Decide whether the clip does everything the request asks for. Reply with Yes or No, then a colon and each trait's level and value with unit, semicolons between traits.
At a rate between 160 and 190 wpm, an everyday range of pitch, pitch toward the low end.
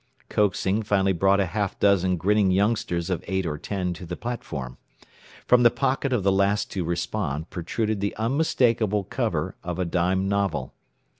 Yes: average, 165 wpm; average, 3.1 semitones; very low, 95 Hz